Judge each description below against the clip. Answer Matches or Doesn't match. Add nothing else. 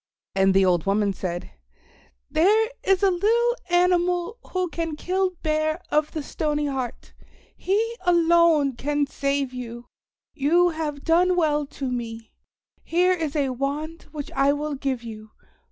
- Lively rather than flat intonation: Doesn't match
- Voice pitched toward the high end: Matches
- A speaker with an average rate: Matches